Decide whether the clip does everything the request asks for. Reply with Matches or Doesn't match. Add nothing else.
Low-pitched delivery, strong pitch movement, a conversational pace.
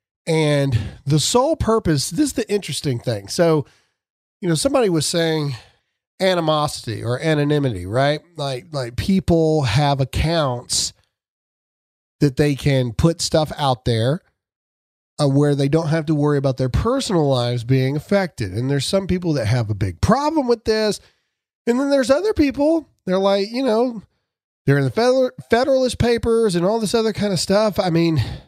Doesn't match